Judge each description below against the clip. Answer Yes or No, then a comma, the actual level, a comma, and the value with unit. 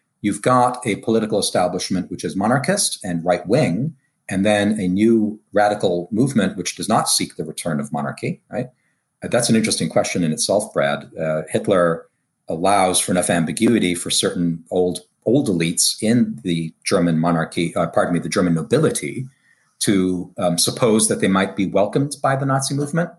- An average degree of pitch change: No, wide, 6.3 semitones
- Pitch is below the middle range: Yes, low, 105 Hz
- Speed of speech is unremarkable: Yes, average, 170 wpm